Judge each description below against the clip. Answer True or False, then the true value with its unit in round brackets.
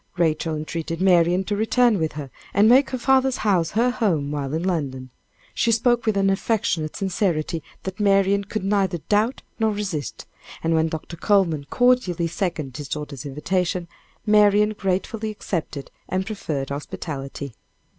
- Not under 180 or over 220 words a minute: False (150 wpm)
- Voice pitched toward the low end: False (185 Hz)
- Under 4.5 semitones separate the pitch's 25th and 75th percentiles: False (5.1 semitones)